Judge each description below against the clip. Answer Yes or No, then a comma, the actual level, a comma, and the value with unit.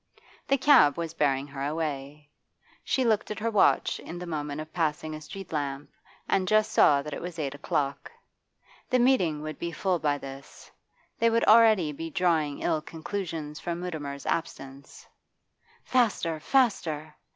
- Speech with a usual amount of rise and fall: Yes, average, 4.2 semitones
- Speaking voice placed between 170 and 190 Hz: No, medium, 160 Hz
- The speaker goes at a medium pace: Yes, average, 160 wpm